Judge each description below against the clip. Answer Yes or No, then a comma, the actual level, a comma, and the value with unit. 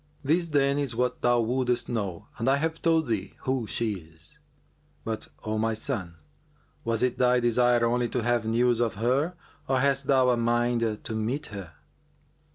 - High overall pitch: No, low, 120 Hz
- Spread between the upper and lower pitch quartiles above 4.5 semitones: No, average, 2.8 semitones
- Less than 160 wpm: No, average, 175 wpm